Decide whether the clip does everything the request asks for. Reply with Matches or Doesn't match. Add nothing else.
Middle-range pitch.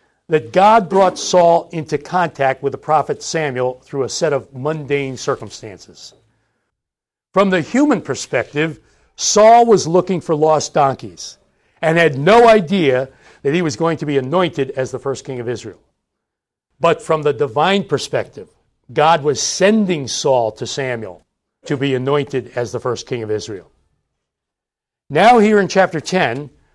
Matches